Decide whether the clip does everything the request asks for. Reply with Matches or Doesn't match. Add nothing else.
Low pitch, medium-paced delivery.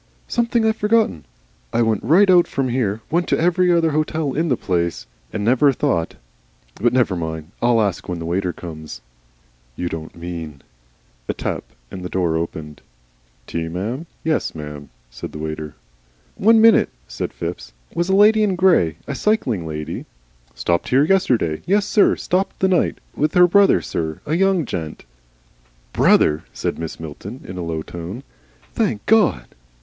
Matches